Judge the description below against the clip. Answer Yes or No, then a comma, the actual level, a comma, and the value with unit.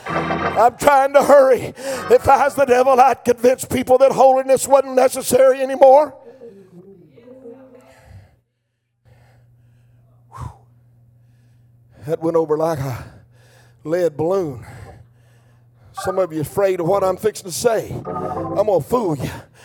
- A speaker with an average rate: No, slow, 120 wpm